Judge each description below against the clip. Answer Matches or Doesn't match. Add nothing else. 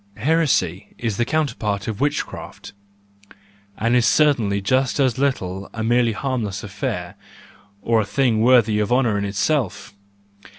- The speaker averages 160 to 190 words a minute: Doesn't match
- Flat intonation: Doesn't match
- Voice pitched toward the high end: Doesn't match